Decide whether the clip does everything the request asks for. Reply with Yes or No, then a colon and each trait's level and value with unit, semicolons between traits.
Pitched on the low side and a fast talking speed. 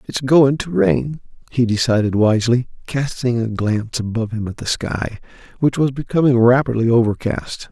No: low, 120 Hz; average, 155 wpm